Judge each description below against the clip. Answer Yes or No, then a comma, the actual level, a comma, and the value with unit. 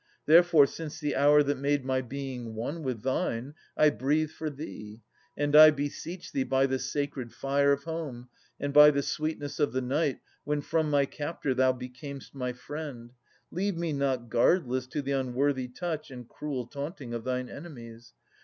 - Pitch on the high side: No, medium, 140 Hz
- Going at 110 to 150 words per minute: No, average, 175 wpm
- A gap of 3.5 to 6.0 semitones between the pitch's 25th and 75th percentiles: No, average, 2.8 semitones